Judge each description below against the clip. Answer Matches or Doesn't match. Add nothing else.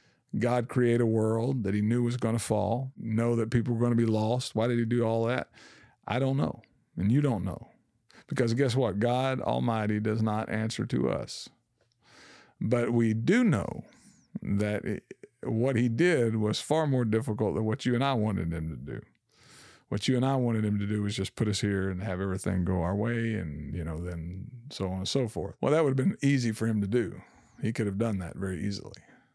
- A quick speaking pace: Matches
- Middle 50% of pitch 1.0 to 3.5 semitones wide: Matches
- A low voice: Matches